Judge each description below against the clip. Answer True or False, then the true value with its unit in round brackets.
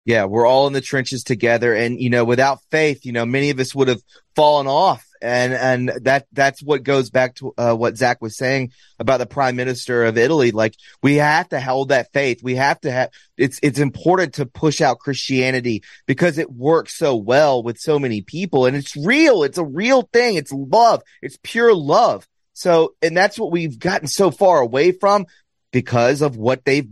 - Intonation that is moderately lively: True (3.8 semitones)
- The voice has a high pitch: False (135 Hz)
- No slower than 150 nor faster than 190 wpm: False (205 wpm)